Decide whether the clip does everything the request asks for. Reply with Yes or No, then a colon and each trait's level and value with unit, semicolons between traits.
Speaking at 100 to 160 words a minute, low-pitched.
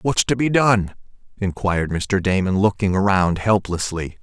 Yes: average, 140 wpm; low, 100 Hz